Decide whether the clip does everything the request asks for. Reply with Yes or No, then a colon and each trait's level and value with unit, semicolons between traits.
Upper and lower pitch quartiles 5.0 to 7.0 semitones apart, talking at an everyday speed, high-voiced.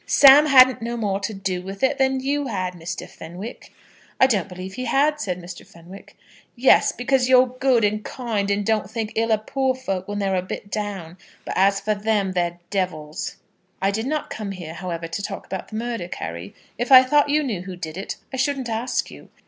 No: wide, 5.5 semitones; fast, 215 wpm; high, 210 Hz